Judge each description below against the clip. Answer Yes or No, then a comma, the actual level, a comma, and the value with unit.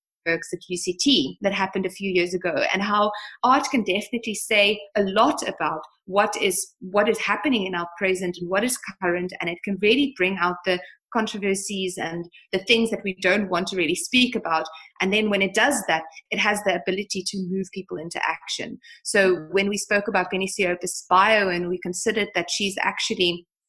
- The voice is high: Yes, high, 195 Hz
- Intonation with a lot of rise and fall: No, narrow, 2.5 semitones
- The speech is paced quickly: No, average, 195 wpm